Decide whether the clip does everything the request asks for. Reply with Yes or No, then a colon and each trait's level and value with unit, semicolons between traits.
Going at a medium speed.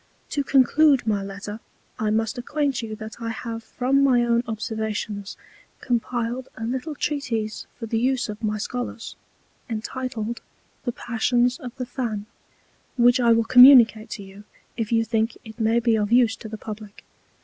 Yes: average, 165 wpm